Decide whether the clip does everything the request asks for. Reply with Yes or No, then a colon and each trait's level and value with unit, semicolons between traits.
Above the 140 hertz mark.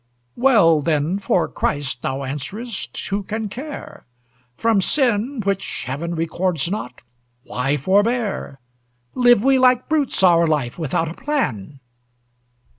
Yes: high, 190 Hz